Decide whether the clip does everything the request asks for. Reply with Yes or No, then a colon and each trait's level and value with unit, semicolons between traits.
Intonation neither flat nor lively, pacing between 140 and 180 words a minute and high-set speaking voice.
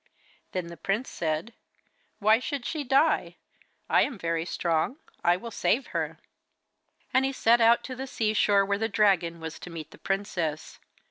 No: wide, 6.0 semitones; average, 175 wpm; high, 200 Hz